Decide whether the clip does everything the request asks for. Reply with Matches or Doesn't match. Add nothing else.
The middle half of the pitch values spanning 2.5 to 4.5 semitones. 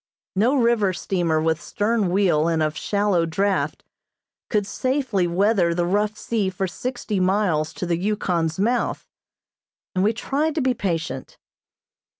Matches